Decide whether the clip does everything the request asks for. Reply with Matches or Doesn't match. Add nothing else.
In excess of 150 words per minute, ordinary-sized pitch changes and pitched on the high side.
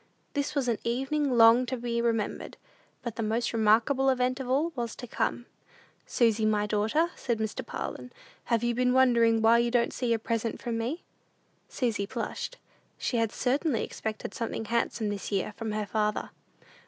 Doesn't match